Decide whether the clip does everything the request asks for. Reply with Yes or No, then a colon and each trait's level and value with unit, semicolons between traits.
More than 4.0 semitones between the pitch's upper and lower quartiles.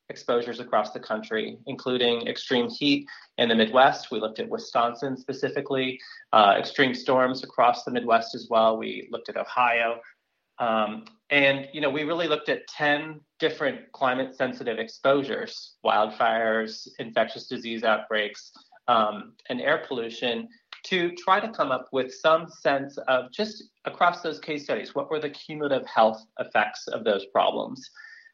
Yes: average, 4.4 semitones